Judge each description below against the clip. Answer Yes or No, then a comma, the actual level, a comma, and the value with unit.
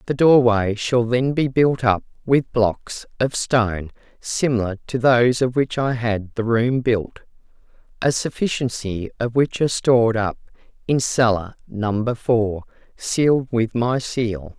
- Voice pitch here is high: No, low, 120 Hz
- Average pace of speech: Yes, average, 150 wpm